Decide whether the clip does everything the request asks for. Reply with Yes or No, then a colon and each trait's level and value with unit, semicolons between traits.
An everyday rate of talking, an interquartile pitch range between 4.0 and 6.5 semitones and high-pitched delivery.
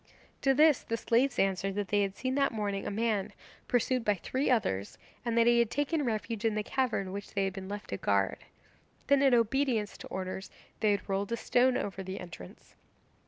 No: fast, 210 wpm; average, 4.3 semitones; high, 215 Hz